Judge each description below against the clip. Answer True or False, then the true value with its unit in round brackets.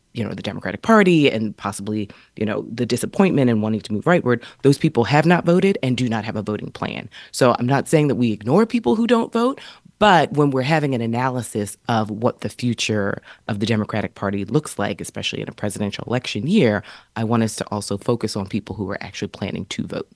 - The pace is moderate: False (225 wpm)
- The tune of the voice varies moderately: False (5.9 semitones)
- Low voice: True (120 Hz)